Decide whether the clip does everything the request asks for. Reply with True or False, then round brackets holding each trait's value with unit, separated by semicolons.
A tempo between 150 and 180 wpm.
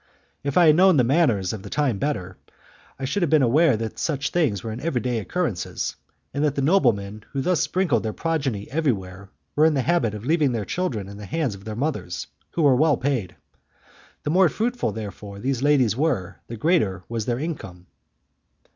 False (200 wpm)